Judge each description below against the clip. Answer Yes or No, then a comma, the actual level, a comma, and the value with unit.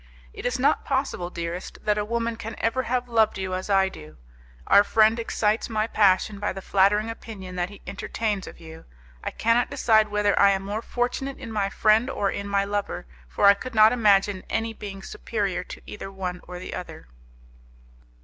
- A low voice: No, high, 210 Hz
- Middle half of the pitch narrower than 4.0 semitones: Yes, average, 2.8 semitones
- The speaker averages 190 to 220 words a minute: Yes, average, 195 wpm